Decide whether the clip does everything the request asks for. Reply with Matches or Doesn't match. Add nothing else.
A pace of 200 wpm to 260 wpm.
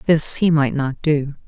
Matches